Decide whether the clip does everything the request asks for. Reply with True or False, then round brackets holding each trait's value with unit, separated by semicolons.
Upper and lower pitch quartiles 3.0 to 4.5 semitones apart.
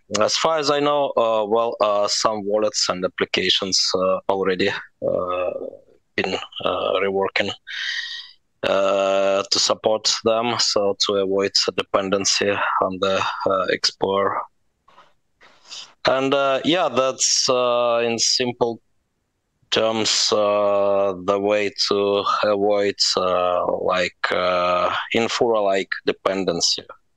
True (3.6 semitones)